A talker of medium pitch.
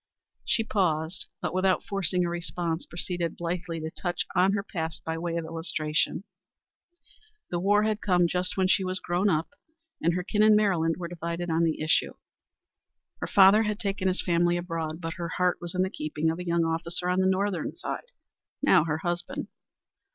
Yes: medium, 175 Hz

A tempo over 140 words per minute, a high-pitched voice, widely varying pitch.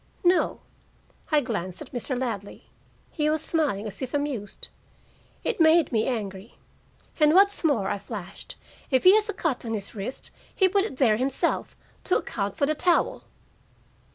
Yes: average, 165 wpm; very high, 260 Hz; wide, 6.9 semitones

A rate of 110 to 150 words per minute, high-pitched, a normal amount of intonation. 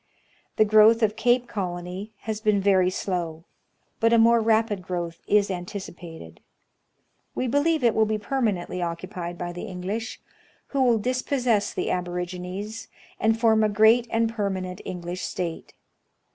Yes: average, 145 wpm; high, 205 Hz; average, 3.9 semitones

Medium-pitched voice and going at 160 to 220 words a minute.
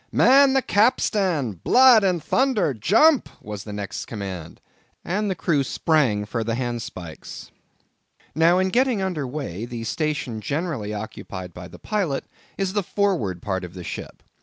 No: medium, 145 Hz; average, 145 wpm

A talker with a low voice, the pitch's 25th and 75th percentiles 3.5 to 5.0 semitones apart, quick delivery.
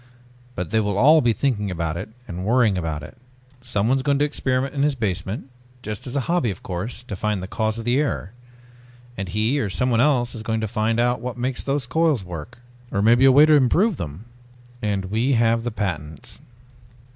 Yes: low, 115 Hz; average, 4.6 semitones; fast, 210 wpm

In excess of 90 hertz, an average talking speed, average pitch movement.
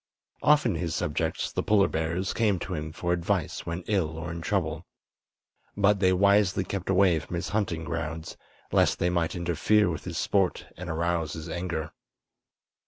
No: very low, 85 Hz; average, 170 wpm; average, 3.1 semitones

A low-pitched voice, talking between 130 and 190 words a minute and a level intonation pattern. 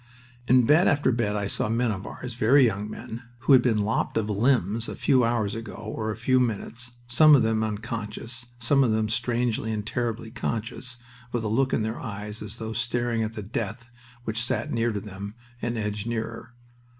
No: low, 115 Hz; average, 200 wpm; narrow, 2.0 semitones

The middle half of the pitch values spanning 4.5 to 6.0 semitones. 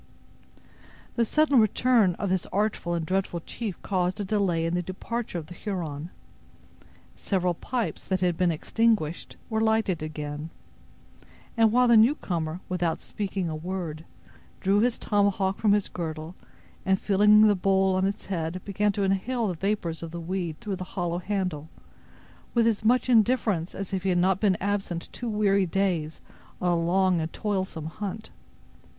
No: average, 3.4 semitones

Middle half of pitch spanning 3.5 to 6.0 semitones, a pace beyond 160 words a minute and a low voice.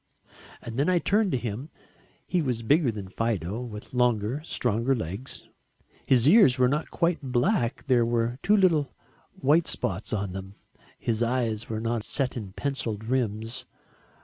No: average, 4.1 semitones; average, 155 wpm; low, 120 Hz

